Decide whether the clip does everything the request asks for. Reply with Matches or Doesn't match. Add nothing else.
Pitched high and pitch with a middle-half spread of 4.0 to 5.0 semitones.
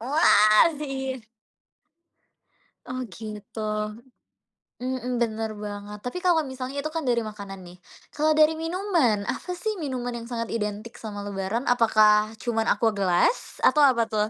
Matches